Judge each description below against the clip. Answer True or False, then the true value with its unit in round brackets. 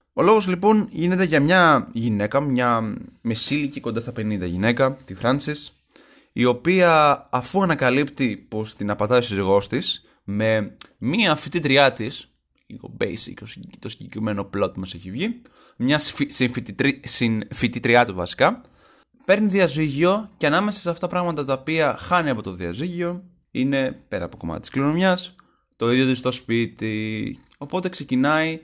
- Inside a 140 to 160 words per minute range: True (150 wpm)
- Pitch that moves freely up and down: True (6.8 semitones)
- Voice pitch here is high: False (135 Hz)